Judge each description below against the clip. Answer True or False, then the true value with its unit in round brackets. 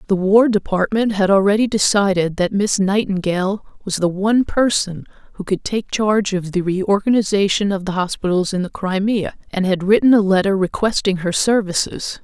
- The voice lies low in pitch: False (195 Hz)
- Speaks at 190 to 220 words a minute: False (165 wpm)